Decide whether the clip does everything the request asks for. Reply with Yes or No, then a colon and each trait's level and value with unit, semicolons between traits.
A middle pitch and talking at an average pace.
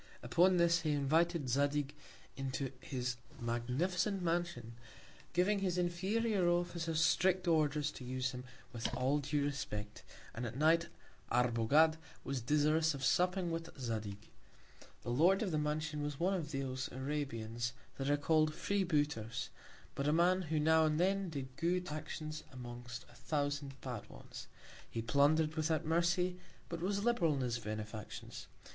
Yes: medium, 150 Hz; average, 150 wpm